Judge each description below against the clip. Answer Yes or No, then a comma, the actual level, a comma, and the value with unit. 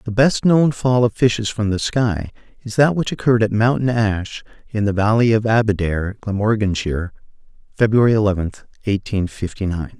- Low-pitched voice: Yes, low, 110 Hz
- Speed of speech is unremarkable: Yes, average, 160 wpm